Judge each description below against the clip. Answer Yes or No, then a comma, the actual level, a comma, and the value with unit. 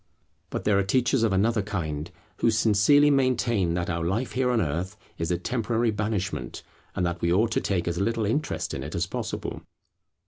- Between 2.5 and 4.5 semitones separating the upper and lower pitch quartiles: No, average, 5.0 semitones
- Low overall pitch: Yes, low, 105 Hz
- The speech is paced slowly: No, average, 195 wpm